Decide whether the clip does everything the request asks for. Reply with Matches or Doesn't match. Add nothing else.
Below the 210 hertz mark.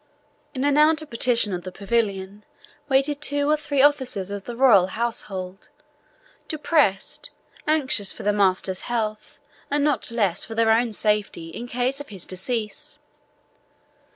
Doesn't match